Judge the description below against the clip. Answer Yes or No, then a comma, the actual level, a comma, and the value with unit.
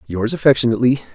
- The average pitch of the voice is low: Yes, low, 115 Hz